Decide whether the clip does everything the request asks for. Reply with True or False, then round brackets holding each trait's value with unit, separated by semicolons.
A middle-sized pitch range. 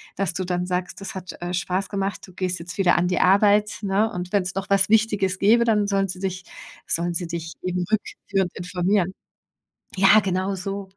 False (1.8 semitones)